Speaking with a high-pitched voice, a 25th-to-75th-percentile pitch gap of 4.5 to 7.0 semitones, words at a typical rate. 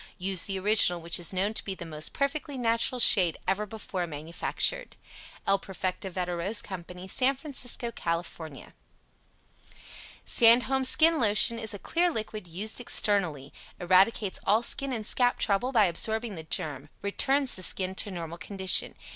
Yes: high, 200 Hz; average, 4.8 semitones; average, 155 wpm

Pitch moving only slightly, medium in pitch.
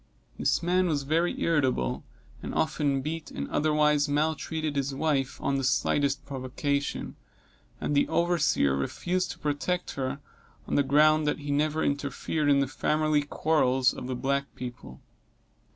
Yes: narrow, 2.3 semitones; medium, 145 Hz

